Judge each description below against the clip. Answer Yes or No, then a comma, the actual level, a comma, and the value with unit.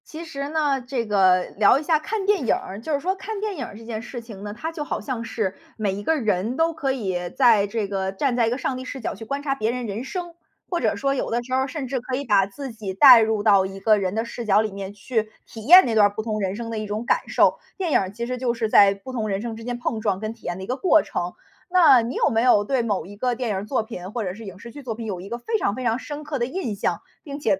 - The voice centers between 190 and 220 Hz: No, high, 230 Hz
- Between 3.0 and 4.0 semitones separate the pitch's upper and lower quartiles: No, average, 4.8 semitones